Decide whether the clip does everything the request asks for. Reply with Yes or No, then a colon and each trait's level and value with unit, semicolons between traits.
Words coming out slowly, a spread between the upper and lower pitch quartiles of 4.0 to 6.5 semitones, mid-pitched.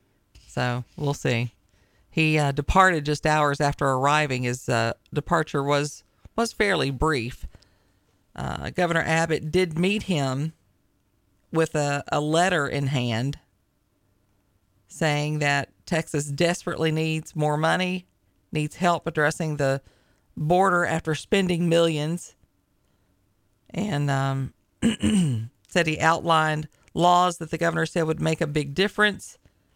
Yes: slow, 120 wpm; average, 5.0 semitones; medium, 150 Hz